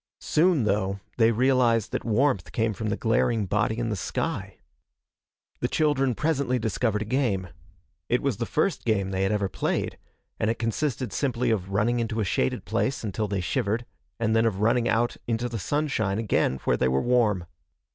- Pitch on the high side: No, low, 115 Hz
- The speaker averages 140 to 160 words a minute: No, average, 185 wpm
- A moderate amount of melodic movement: Yes, average, 3.2 semitones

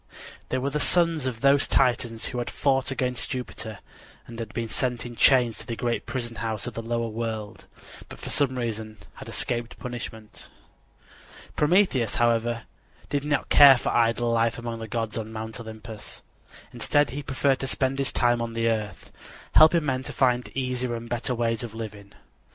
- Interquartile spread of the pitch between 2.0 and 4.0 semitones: Yes, narrow, 2.4 semitones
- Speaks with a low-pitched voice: Yes, low, 120 Hz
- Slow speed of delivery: No, average, 180 wpm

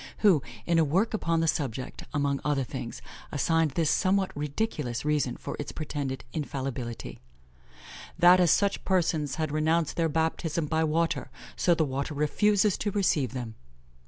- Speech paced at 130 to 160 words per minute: Yes, average, 155 wpm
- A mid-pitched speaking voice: Yes, medium, 155 Hz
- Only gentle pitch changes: No, average, 3.2 semitones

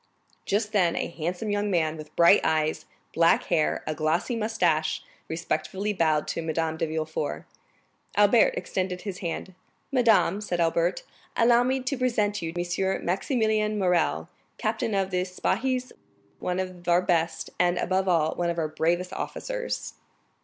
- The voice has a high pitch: No, medium, 180 Hz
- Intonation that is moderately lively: Yes, average, 4.1 semitones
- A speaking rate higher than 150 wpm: No, average, 145 wpm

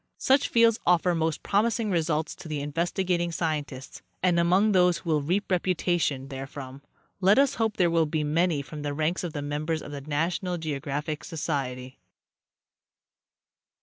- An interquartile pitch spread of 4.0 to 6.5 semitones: No, average, 3.6 semitones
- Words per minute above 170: No, average, 155 wpm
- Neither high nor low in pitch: Yes, medium, 165 Hz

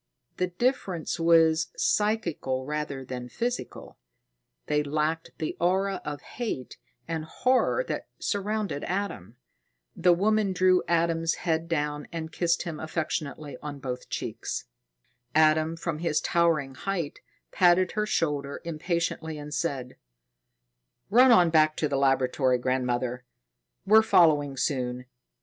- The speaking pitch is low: No, medium, 160 Hz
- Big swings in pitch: No, average, 3.9 semitones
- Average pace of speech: No, slow, 125 wpm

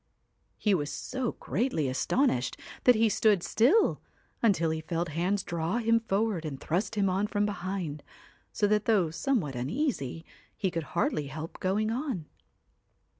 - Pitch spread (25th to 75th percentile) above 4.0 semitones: Yes, wide, 5.6 semitones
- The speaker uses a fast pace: No, average, 150 wpm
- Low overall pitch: No, high, 190 Hz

